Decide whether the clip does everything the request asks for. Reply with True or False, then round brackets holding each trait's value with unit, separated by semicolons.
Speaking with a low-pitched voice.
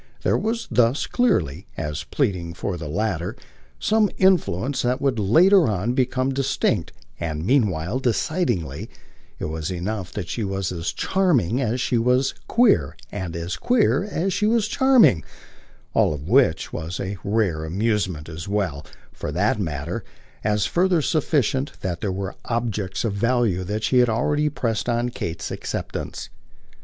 True (110 Hz)